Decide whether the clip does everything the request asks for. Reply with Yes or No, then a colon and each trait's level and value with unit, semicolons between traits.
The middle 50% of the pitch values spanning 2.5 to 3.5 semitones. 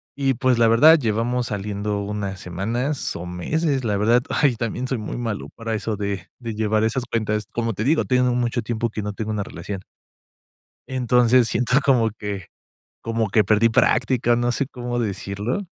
Yes: average, 2.8 semitones